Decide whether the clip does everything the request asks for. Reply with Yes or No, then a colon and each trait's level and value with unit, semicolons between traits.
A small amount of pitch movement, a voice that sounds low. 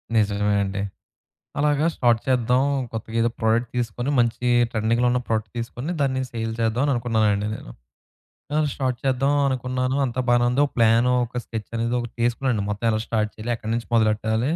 Yes: narrow, 2.2 semitones; low, 115 Hz